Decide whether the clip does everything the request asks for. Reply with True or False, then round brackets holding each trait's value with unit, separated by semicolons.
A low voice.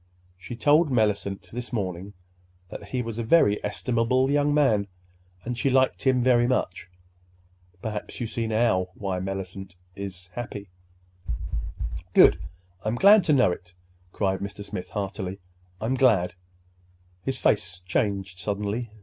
True (105 Hz)